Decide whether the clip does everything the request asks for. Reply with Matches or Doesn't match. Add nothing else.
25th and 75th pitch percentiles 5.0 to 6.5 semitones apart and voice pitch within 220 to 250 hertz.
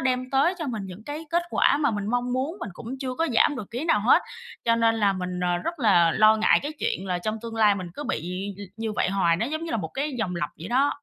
Matches